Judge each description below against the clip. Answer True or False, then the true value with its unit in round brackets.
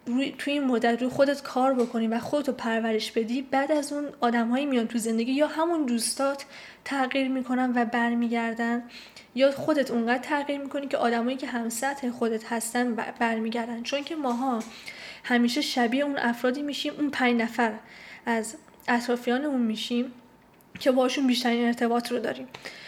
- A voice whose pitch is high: True (245 Hz)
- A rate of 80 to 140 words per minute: False (155 wpm)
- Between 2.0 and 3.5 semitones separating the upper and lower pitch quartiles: True (2.8 semitones)